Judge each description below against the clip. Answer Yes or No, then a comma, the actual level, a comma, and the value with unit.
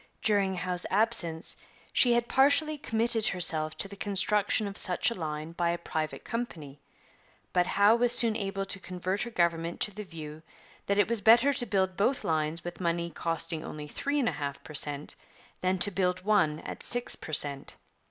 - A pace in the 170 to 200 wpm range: Yes, average, 190 wpm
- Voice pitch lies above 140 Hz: Yes, medium, 185 Hz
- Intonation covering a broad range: No, average, 5.0 semitones